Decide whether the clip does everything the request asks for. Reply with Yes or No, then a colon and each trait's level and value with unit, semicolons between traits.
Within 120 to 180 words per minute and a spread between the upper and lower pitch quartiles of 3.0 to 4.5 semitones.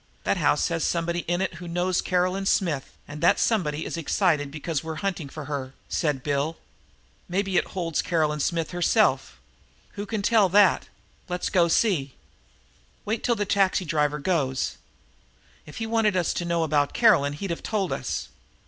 Yes: average, 165 wpm; average, 4.2 semitones